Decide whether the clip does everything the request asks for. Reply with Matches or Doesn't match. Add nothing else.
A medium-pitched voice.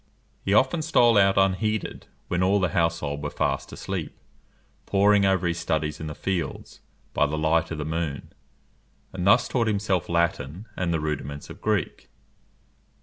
Doesn't match